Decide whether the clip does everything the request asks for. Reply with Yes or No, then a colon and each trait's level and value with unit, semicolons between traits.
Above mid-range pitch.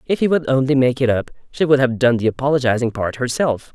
No: low, 130 Hz